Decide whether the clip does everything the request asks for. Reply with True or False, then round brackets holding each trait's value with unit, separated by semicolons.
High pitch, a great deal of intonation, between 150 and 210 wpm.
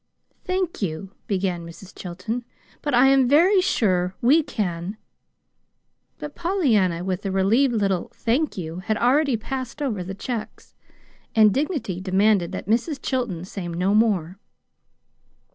False (215 Hz; 6.4 semitones; 140 wpm)